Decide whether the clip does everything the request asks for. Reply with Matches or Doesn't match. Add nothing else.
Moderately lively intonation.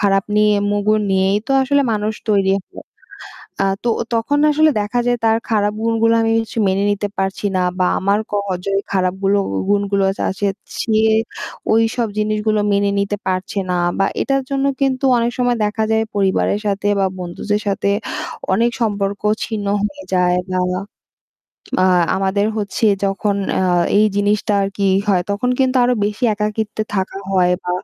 Doesn't match